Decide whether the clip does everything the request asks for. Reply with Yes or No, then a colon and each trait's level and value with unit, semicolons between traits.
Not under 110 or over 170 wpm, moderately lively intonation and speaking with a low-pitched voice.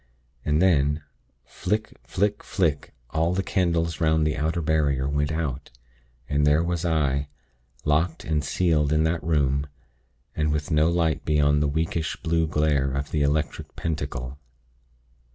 No: average, 145 wpm; narrow, 2.1 semitones; very low, 75 Hz